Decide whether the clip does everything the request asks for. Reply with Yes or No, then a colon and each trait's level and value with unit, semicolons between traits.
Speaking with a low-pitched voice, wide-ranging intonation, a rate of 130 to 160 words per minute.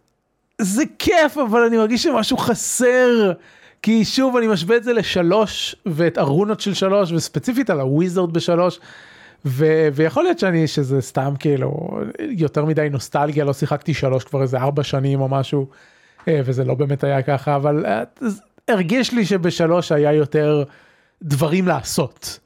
No: medium, 170 Hz; wide, 7.1 semitones; average, 145 wpm